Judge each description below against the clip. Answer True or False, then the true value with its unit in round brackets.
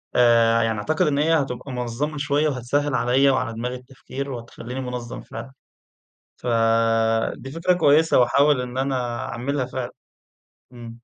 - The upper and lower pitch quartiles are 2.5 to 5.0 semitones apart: True (3.1 semitones)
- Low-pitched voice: True (125 Hz)